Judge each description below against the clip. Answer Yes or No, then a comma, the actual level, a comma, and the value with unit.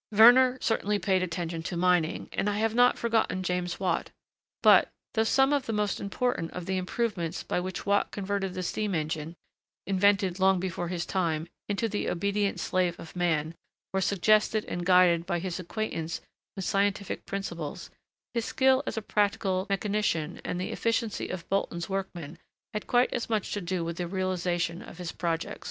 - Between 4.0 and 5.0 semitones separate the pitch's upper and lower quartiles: No, average, 3.2 semitones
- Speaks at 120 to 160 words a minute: No, average, 175 wpm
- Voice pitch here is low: No, high, 190 Hz